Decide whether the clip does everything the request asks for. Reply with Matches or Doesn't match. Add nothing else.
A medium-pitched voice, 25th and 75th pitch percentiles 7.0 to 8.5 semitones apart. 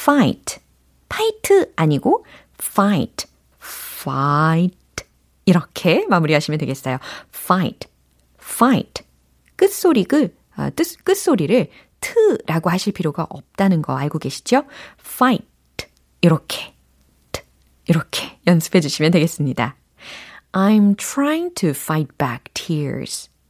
Matches